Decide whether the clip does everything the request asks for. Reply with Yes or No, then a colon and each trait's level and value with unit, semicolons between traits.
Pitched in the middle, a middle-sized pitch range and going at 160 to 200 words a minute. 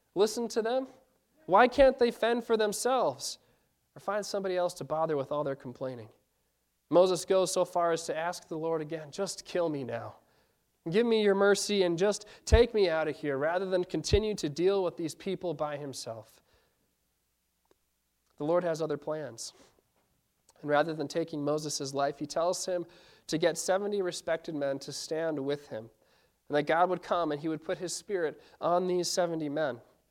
Yes: medium, 170 Hz; average, 4.6 semitones; average, 185 wpm